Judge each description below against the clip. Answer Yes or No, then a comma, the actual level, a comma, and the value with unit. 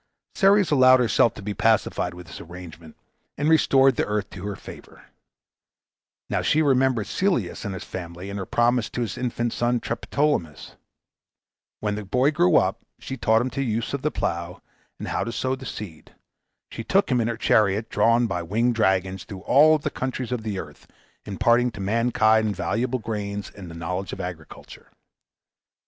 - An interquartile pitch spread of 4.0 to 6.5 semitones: Yes, average, 4.8 semitones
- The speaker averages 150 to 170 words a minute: No, average, 180 wpm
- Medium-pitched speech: No, low, 110 Hz